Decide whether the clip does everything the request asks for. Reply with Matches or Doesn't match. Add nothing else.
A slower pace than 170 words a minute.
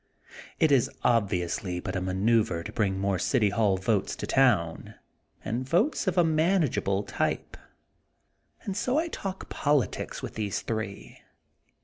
Matches